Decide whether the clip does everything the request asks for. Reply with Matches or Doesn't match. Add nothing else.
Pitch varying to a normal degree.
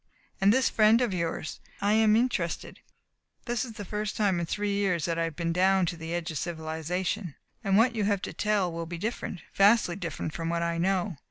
Matches